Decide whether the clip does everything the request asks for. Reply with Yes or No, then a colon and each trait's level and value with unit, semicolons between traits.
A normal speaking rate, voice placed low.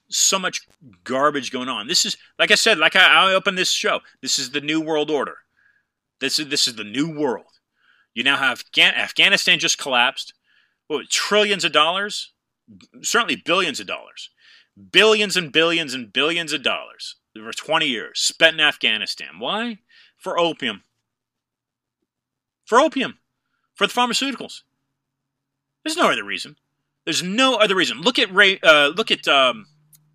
No: average, 155 wpm; medium, 160 Hz